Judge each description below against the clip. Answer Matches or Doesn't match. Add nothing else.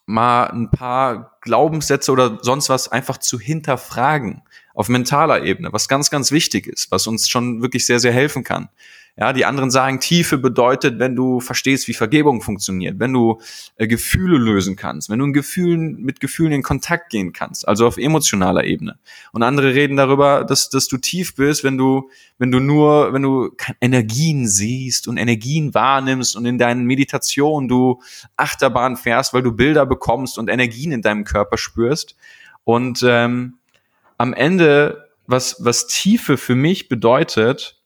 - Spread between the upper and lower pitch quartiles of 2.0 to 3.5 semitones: Matches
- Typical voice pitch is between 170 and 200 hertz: Doesn't match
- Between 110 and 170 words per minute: Matches